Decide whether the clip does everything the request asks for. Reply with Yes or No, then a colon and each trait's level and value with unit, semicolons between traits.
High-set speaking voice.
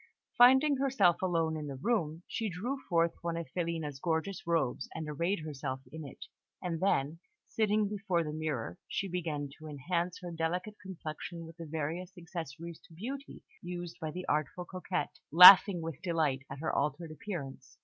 No: medium, 170 Hz